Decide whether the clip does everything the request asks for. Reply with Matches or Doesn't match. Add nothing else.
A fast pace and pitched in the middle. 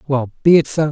Matches